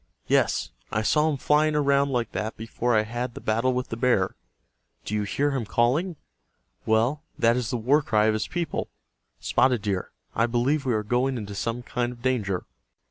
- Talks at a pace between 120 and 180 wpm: No, average, 190 wpm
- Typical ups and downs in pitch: Yes, average, 3.6 semitones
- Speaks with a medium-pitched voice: No, low, 120 Hz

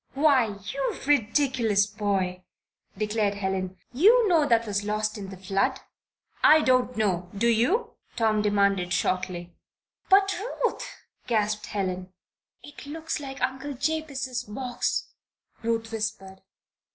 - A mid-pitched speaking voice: No, high, 225 Hz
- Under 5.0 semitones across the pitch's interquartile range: No, wide, 5.5 semitones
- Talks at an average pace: No, slow, 120 wpm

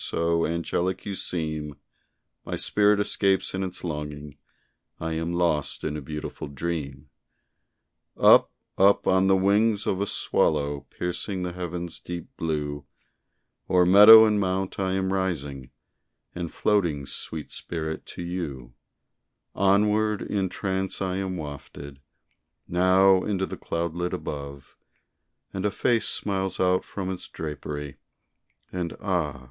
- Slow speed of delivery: Yes, slow, 130 wpm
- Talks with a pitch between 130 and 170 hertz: No, very low, 90 Hz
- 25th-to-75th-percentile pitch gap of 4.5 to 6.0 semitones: No, average, 3.9 semitones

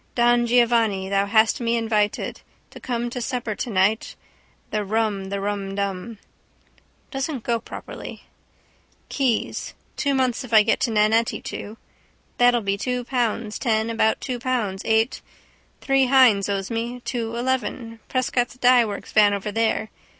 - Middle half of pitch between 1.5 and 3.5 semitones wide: Yes, average, 2.7 semitones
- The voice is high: Yes, high, 230 Hz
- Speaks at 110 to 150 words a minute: Yes, slow, 135 wpm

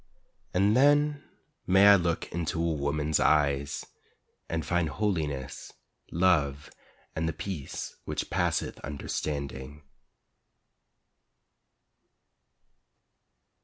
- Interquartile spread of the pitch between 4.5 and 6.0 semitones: No, average, 4.1 semitones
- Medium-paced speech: No, slow, 85 wpm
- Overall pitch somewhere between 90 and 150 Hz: No, very low, 80 Hz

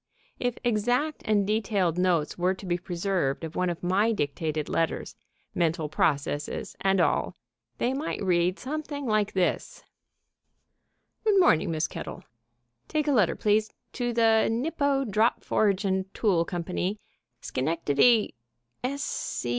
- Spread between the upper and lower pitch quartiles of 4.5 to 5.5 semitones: Yes, average, 5.2 semitones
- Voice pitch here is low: No, high, 195 Hz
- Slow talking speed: Yes, slow, 130 wpm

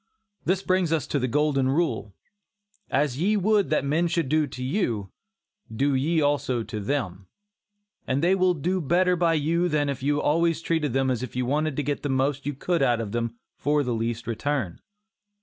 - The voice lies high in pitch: No, medium, 145 Hz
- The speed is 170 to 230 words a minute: Yes, average, 200 wpm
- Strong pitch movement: No, average, 4.5 semitones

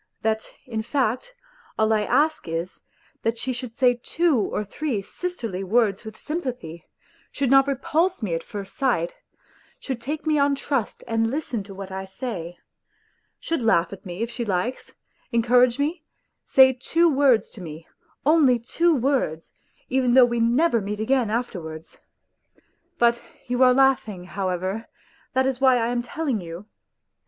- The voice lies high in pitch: Yes, high, 240 Hz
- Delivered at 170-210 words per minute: No, average, 160 wpm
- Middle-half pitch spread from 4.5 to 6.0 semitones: Yes, average, 4.8 semitones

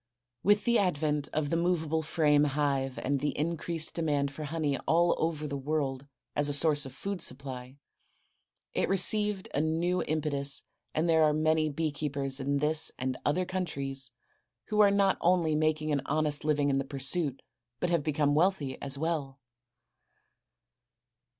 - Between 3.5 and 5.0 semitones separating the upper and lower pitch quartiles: No, average, 2.8 semitones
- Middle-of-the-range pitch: Yes, medium, 150 Hz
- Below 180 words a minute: Yes, average, 160 wpm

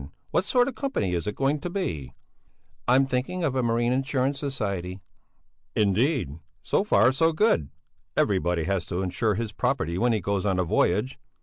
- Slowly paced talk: No, average, 180 wpm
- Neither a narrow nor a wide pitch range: No, wide, 6.5 semitones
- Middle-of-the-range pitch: No, low, 115 Hz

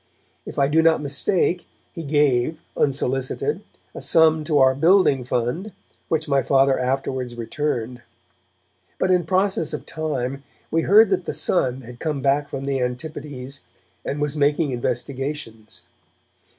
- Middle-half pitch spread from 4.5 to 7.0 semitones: No, average, 3.6 semitones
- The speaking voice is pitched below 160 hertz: Yes, medium, 140 Hz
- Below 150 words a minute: Yes, average, 140 wpm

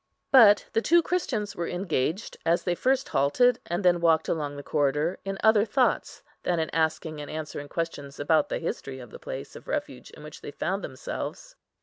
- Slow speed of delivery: No, average, 195 wpm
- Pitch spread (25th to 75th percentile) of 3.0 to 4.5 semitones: No, wide, 5.5 semitones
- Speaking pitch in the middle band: Yes, medium, 165 Hz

